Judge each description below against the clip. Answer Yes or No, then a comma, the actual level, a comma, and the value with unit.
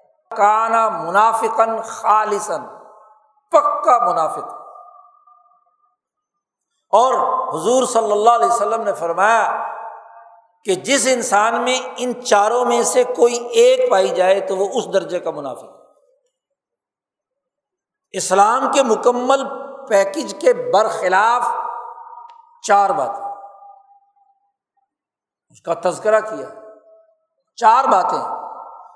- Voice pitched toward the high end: Yes, high, 240 Hz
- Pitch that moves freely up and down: Yes, wide, 7.2 semitones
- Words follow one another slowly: Yes, slow, 95 wpm